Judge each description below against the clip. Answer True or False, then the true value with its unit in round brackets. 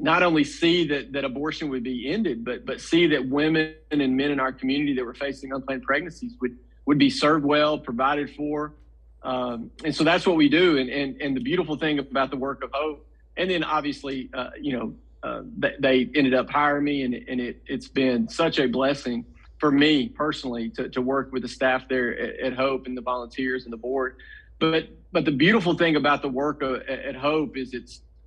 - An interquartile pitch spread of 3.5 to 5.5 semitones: False (2.7 semitones)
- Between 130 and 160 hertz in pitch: True (135 Hz)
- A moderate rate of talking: False (215 wpm)